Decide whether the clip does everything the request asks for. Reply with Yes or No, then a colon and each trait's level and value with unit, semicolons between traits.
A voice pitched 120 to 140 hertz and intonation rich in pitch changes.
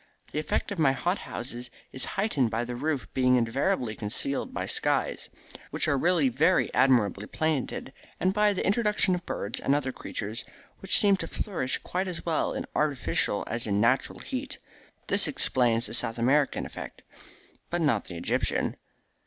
Yes: low, 135 Hz; wide, 6.4 semitones